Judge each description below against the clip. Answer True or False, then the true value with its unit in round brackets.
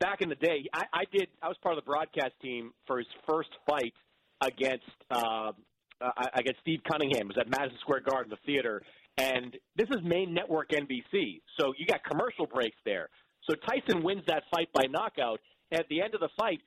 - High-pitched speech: False (140 Hz)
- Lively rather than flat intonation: False (4.8 semitones)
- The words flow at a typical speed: False (210 wpm)